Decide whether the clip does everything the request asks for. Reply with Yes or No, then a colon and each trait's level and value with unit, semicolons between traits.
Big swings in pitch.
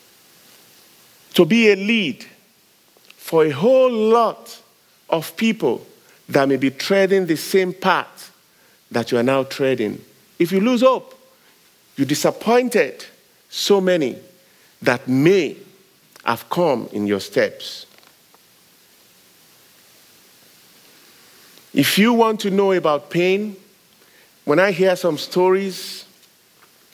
Yes: wide, 6.2 semitones